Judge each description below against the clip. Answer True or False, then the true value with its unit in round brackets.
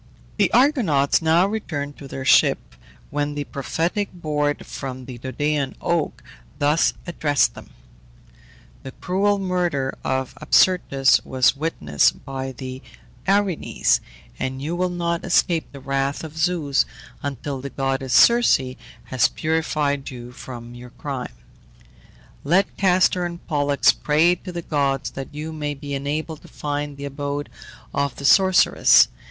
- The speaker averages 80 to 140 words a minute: True (135 wpm)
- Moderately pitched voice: True (145 Hz)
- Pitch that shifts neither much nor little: True (4.1 semitones)